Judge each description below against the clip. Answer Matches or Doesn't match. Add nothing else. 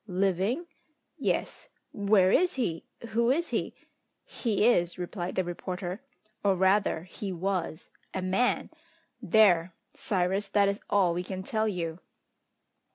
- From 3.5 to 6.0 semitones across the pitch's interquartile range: Doesn't match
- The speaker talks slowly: Matches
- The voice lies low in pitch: Doesn't match